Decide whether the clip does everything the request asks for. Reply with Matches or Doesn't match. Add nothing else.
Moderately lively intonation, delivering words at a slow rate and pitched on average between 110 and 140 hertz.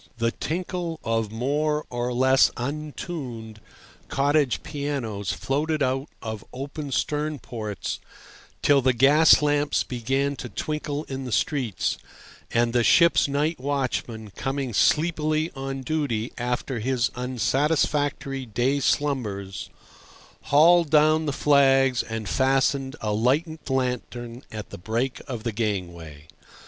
Matches